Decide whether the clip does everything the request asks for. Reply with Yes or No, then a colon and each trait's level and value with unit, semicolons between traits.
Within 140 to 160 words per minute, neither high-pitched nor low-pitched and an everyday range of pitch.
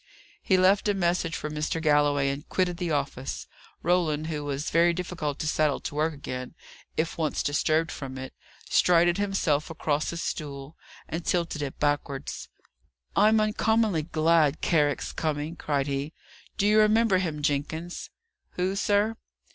Yes: average, 150 wpm; medium, 160 Hz; average, 3.5 semitones